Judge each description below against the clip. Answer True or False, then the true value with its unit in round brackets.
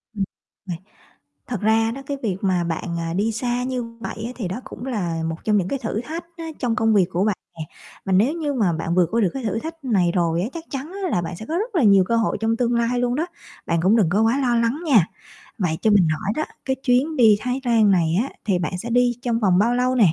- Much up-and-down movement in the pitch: False (5.0 semitones)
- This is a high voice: True (225 Hz)